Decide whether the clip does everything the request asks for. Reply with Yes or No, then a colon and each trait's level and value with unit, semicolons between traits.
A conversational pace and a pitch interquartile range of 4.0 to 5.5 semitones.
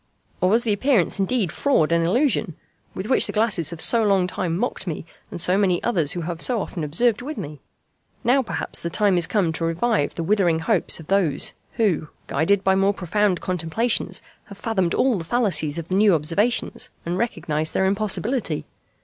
Yes: average, 190 wpm; average, 4.7 semitones